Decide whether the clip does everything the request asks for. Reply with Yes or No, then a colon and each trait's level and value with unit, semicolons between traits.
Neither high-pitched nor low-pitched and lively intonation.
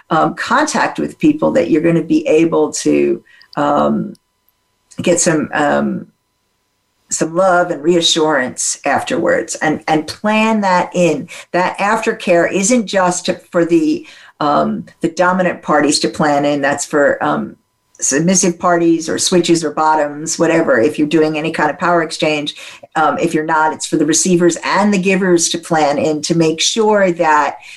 No: medium, 165 Hz; average, 2.8 semitones